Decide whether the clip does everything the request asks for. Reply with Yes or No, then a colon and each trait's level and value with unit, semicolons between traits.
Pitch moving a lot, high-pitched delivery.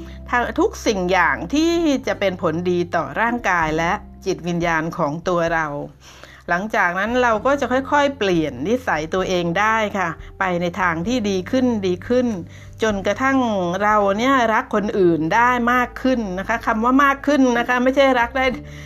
Yes: wide, 6.0 semitones; high, 205 Hz